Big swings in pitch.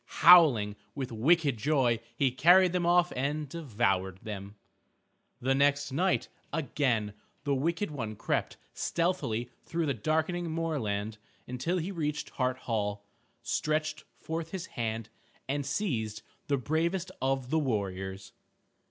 Yes: wide, 6.7 semitones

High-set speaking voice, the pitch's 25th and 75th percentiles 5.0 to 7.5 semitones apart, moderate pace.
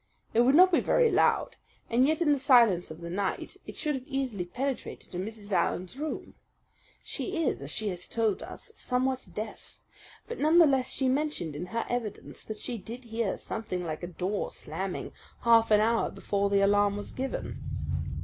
Yes: high, 225 Hz; wide, 5.4 semitones; average, 190 wpm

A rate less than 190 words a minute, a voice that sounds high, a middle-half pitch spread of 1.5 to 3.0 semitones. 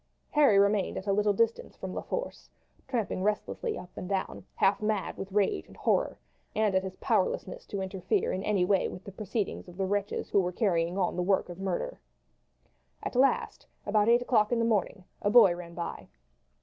No: average, 200 wpm; high, 200 Hz; narrow, 2.5 semitones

